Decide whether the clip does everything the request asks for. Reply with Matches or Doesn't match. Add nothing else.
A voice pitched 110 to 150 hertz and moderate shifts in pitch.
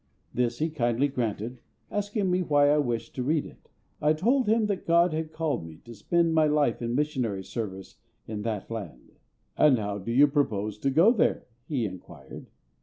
Doesn't match